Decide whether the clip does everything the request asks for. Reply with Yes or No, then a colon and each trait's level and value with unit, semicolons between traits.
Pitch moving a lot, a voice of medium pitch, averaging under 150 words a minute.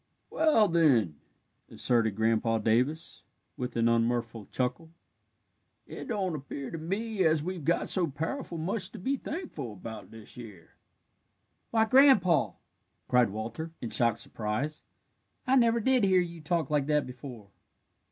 Yes: wide, 8.0 semitones; medium, 150 Hz; average, 140 wpm